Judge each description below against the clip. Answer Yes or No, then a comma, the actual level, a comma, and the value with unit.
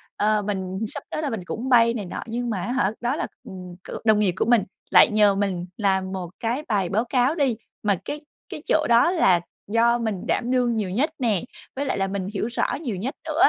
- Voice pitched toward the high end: Yes, high, 225 Hz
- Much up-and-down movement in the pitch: No, average, 4.1 semitones